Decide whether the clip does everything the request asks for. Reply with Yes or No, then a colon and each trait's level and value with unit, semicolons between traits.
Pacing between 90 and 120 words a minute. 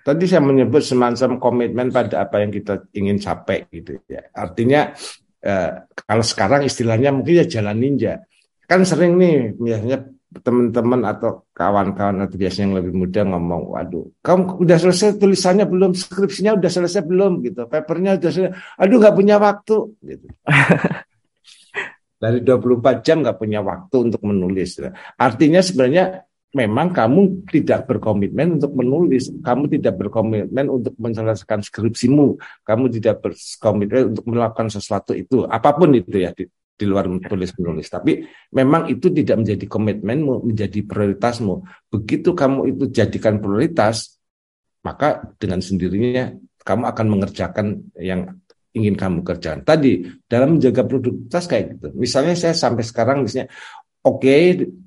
No: fast, 140 wpm